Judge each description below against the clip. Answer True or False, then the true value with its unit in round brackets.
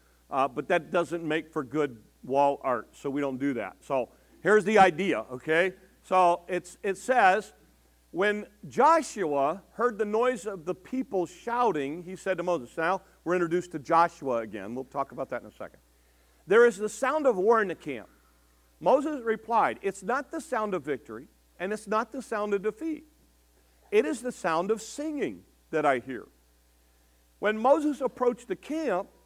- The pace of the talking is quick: False (180 wpm)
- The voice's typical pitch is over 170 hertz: True (185 Hz)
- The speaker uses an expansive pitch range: True (8.1 semitones)